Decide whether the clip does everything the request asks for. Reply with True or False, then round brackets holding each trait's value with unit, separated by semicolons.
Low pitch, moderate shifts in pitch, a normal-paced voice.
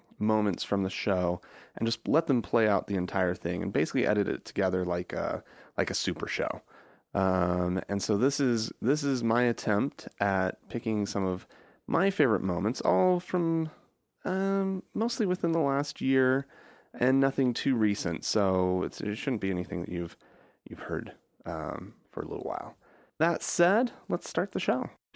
False (110 Hz; 6.8 semitones; 175 wpm)